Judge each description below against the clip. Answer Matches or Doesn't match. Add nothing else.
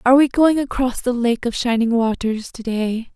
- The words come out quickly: Doesn't match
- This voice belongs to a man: Doesn't match